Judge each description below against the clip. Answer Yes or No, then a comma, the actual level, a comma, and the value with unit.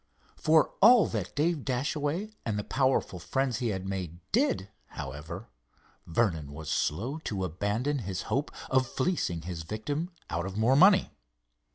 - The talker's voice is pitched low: Yes, low, 115 Hz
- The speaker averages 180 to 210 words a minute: No, average, 150 wpm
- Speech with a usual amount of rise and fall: No, wide, 8.1 semitones